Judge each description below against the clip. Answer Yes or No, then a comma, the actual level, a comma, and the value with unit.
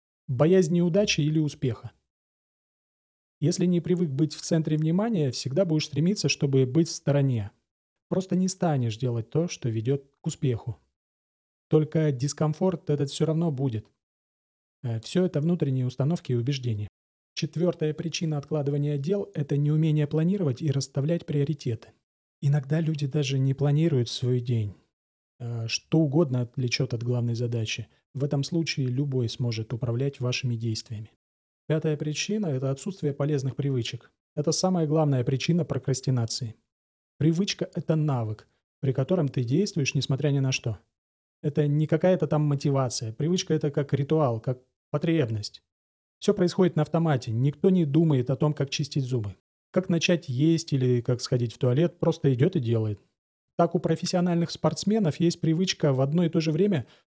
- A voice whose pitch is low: No, medium, 145 Hz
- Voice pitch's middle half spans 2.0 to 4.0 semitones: No, average, 4.6 semitones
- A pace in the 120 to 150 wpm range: Yes, average, 145 wpm